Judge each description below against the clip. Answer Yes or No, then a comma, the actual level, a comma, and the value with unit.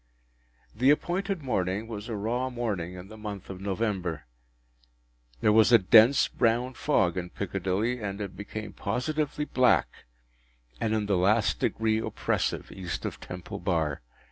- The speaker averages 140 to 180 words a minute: Yes, average, 145 wpm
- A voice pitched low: Yes, low, 105 Hz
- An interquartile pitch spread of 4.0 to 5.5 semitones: Yes, average, 4.3 semitones